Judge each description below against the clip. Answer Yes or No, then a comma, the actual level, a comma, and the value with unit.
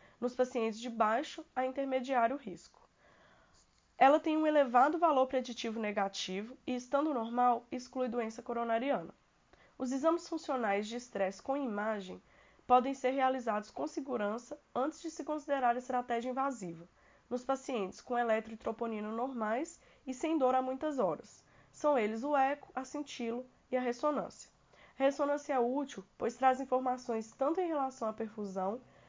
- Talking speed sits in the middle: Yes, average, 145 wpm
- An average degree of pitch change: Yes, average, 3.1 semitones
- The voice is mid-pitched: No, very high, 255 Hz